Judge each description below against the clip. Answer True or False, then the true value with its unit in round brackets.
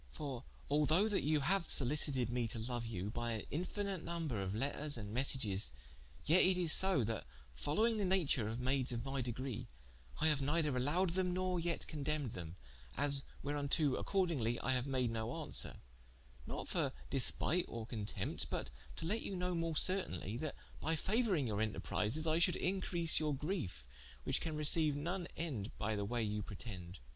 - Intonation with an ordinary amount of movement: False (6.4 semitones)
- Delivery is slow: False (175 wpm)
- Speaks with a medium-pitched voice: True (145 Hz)